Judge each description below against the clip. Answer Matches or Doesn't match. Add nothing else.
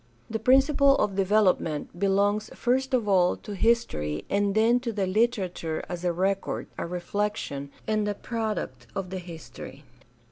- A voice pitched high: Matches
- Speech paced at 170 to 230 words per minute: Doesn't match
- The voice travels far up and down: Doesn't match